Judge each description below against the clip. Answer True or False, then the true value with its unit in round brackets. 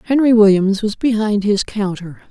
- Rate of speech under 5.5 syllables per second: True (4.9 syllables/s)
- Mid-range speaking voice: False (210 Hz)